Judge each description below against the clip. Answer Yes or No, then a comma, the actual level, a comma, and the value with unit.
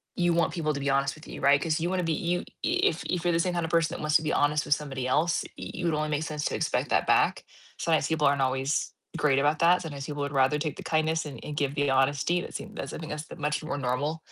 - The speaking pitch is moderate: Yes, medium, 150 Hz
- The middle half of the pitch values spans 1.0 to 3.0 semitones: Yes, narrow, 2.5 semitones